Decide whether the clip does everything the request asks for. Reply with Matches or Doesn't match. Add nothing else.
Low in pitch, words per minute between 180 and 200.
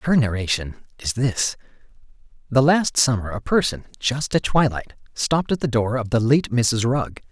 Doesn't match